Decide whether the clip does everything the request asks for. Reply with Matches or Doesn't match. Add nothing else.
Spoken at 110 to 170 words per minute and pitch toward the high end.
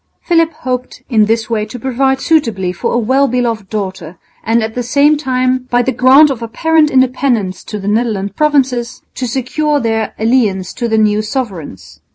Doesn't match